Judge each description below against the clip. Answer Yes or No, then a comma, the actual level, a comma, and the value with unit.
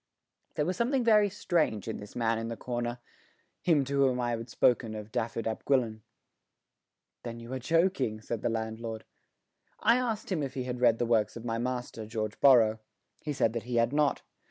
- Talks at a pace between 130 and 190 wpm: No, average, 200 wpm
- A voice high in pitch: No, low, 120 Hz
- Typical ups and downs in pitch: Yes, average, 3.9 semitones